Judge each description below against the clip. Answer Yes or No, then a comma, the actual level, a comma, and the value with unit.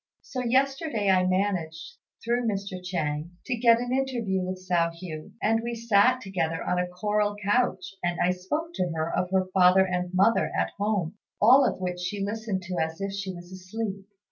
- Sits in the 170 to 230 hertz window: Yes, high, 190 Hz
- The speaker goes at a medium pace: Yes, average, 190 wpm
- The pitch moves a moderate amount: Yes, average, 3.9 semitones